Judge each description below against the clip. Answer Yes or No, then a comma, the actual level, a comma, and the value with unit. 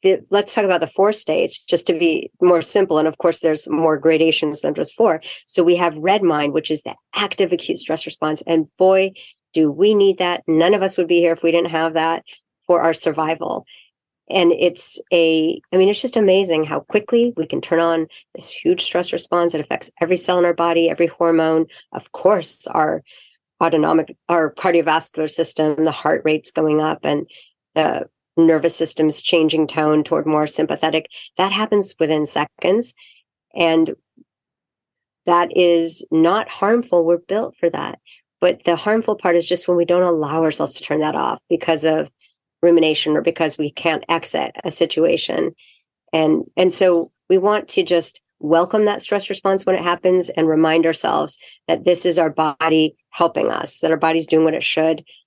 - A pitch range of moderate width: No, narrow, 2.3 semitones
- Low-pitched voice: No, medium, 170 Hz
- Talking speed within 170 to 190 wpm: Yes, average, 185 wpm